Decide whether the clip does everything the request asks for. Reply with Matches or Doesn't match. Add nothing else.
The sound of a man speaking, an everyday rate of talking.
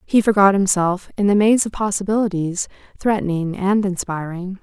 Doesn't match